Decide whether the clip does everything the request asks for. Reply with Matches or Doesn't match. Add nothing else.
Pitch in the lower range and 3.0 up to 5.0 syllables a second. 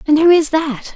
Doesn't match